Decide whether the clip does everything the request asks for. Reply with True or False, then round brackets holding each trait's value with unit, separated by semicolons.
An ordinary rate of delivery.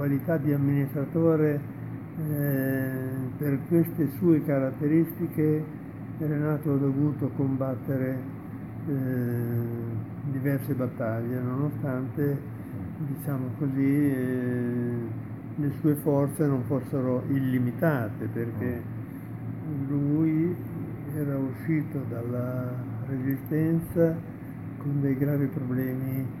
False (80 wpm)